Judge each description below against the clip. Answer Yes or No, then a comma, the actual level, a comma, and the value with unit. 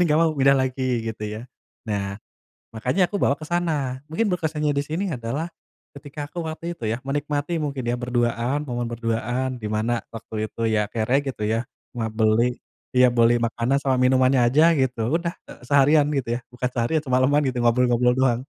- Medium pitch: No, low, 130 Hz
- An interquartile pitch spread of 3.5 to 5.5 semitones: Yes, average, 3.9 semitones